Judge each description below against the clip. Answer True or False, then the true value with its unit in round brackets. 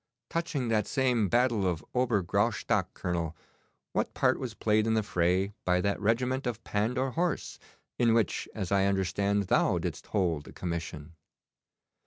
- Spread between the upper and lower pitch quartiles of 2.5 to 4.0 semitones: False (4.6 semitones)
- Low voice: True (105 Hz)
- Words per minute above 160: False (155 wpm)